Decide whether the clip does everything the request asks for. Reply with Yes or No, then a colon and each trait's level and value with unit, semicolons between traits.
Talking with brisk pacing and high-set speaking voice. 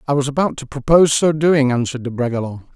No: fast, 220 wpm; low, 135 Hz